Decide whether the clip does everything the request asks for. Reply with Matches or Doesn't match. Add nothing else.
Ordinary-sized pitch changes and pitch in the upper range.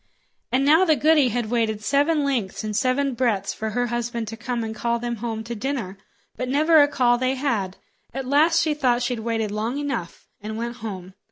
Matches